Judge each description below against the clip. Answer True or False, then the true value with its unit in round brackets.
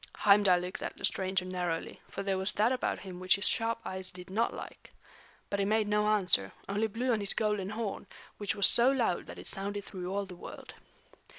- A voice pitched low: False (200 Hz)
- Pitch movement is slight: True (2.3 semitones)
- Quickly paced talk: True (215 wpm)